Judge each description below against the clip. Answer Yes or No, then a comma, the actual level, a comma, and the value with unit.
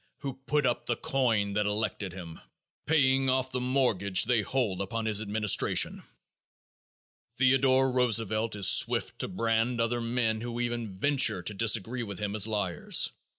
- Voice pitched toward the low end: Yes, low, 115 Hz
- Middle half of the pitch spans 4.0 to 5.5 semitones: No, average, 3.6 semitones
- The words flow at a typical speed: Yes, average, 150 wpm